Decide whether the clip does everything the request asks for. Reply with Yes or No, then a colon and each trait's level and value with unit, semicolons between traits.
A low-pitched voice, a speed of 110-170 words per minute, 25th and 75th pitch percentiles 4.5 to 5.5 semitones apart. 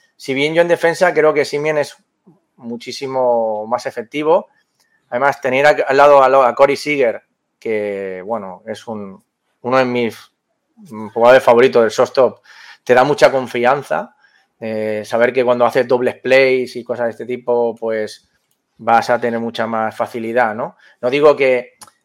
No: low, 125 Hz; average, 160 wpm; average, 3.3 semitones